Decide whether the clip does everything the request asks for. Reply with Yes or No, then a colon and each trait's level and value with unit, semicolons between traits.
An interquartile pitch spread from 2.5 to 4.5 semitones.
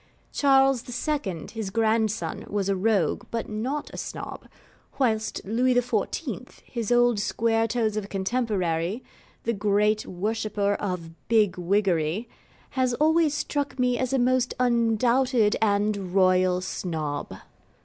Yes: average, 3.8 semitones